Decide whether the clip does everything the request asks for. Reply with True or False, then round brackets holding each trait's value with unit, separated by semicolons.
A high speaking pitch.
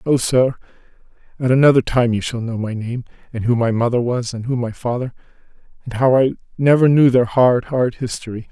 False (125 Hz)